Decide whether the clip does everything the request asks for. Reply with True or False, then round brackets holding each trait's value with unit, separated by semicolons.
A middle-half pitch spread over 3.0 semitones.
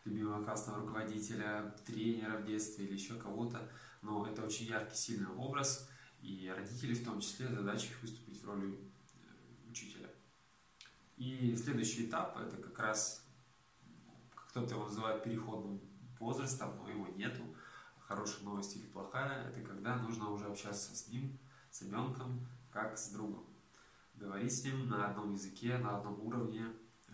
False (2.7 semitones)